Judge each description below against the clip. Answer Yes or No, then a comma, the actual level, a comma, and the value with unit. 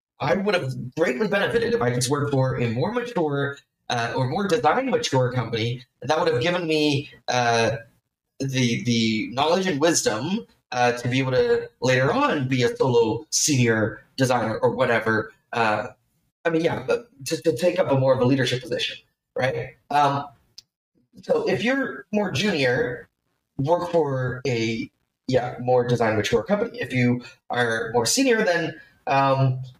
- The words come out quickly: No, average, 165 wpm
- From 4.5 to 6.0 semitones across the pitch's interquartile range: Yes, average, 5.0 semitones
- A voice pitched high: No, low, 135 Hz